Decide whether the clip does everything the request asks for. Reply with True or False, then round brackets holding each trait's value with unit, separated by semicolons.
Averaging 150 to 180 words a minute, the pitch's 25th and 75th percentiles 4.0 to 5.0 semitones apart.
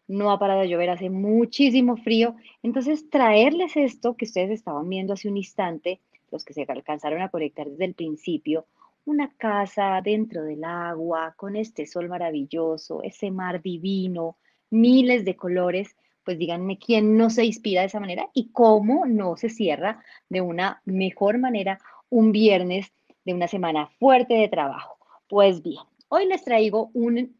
True (160 wpm; 4.4 semitones)